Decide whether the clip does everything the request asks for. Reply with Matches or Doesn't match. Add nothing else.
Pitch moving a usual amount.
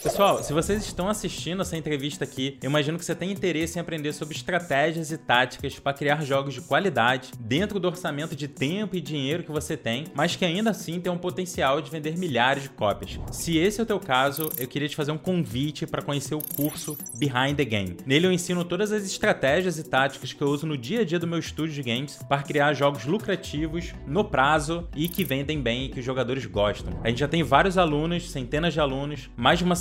Matches